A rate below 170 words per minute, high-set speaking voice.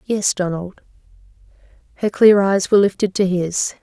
Yes: average, 140 wpm; high, 195 Hz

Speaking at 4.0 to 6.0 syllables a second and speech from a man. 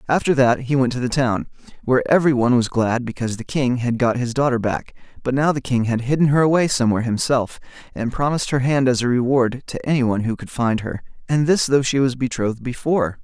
No: 6.3 syllables/s; male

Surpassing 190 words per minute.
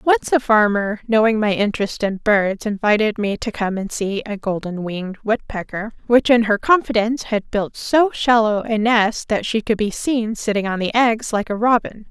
Yes: average, 200 wpm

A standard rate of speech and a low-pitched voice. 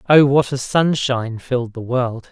Yes: average, 180 wpm; low, 130 Hz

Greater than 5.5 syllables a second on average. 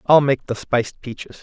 No: 5.3 syllables/s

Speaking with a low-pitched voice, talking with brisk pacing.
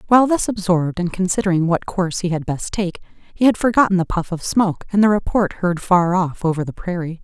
No: medium, 185 Hz; fast, 225 wpm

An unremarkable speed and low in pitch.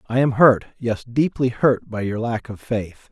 Yes: average, 175 wpm; low, 115 Hz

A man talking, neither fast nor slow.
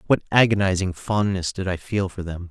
Yes: male; average, 190 wpm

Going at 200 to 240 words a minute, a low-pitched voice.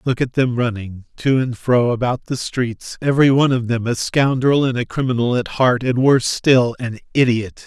Yes: fast, 205 wpm; low, 125 Hz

